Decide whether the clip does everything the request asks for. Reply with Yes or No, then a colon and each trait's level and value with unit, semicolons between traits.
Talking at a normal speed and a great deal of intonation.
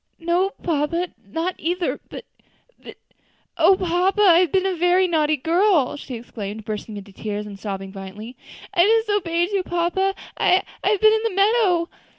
Yes: average, 165 wpm; wide, 7.7 semitones